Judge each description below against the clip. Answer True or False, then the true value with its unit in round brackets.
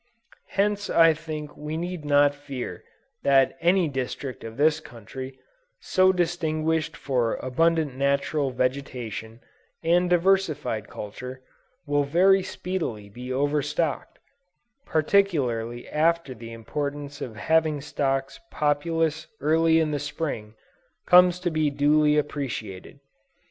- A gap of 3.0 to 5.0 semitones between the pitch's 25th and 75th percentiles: True (3.8 semitones)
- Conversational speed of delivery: False (110 wpm)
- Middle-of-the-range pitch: True (145 Hz)